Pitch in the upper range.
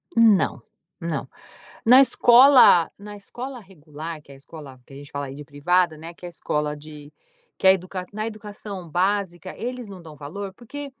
No: medium, 180 Hz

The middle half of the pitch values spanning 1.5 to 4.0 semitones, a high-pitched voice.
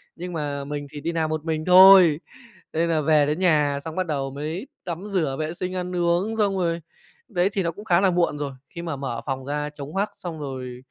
No: average, 3.5 semitones; medium, 160 Hz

